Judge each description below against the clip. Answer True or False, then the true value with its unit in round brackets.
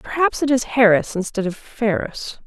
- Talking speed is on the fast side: False (170 wpm)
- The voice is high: True (220 Hz)